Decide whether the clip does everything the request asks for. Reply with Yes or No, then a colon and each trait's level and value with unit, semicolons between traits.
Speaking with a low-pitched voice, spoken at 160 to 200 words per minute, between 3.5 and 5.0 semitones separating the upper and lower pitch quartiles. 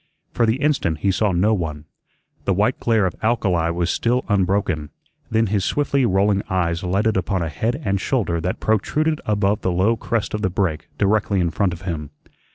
Yes: low, 100 Hz; average, 190 wpm; average, 3.9 semitones